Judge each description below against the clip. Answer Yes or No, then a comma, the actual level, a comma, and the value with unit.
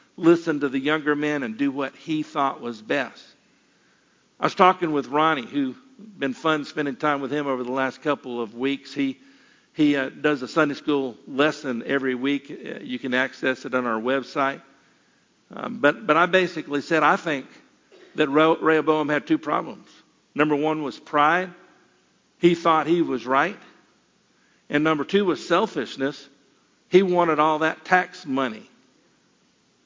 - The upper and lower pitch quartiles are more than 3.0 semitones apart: Yes, average, 3.6 semitones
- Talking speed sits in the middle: Yes, average, 165 wpm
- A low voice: No, medium, 150 Hz